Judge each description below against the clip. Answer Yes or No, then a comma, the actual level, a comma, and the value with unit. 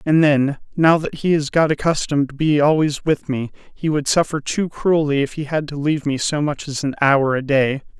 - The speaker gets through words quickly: Yes, fast, 235 wpm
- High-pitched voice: No, medium, 145 Hz